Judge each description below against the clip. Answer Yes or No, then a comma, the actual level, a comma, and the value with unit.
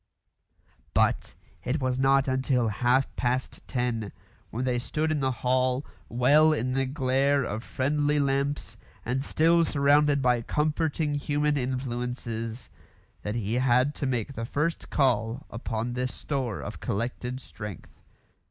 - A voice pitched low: Yes, low, 130 Hz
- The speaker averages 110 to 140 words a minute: Yes, slow, 135 wpm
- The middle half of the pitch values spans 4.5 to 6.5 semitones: No, average, 2.7 semitones